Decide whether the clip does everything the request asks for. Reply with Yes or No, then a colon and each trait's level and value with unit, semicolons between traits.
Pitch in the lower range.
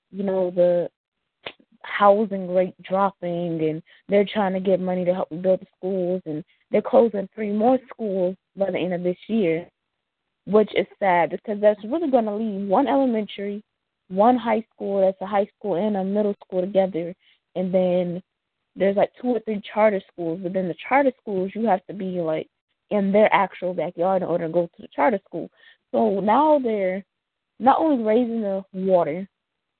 No: high, 195 Hz